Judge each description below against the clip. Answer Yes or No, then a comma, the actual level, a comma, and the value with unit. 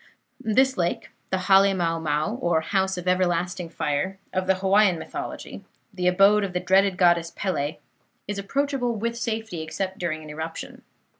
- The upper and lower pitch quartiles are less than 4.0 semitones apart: Yes, average, 2.8 semitones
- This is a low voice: No, medium, 185 Hz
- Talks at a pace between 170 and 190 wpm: No, average, 160 wpm